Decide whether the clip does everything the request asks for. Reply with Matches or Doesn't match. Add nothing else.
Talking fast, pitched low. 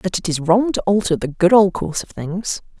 Doesn't match